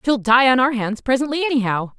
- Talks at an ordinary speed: No, fast, 210 wpm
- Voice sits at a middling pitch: No, very high, 250 Hz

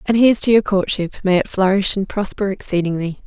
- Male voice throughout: No, female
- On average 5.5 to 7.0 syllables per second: Yes, 6.0 syllables/s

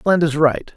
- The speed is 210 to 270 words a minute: Yes, fast, 235 wpm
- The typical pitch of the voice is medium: Yes, medium, 155 Hz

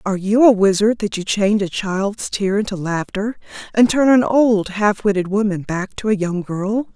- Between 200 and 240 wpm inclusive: Yes, fast, 205 wpm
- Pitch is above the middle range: Yes, high, 205 Hz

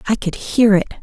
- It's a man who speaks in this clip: No, female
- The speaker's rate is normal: No, fast, 235 wpm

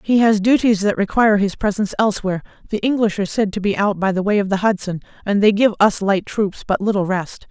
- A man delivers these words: No, female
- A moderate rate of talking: No, fast, 240 wpm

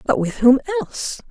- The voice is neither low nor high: No, very high, 280 Hz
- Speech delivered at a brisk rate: No, average, 185 wpm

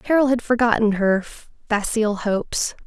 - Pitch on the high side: Yes, high, 225 Hz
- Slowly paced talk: Yes, slow, 125 wpm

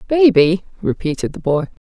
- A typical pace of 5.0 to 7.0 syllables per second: Yes, 5.2 syllables/s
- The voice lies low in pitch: No, medium, 185 Hz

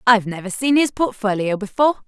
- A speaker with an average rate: Yes, average, 175 wpm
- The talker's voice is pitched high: Yes, high, 225 Hz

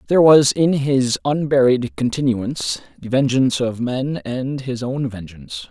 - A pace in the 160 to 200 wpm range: No, average, 145 wpm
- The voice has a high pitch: No, low, 130 Hz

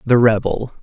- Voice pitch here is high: No, low, 115 Hz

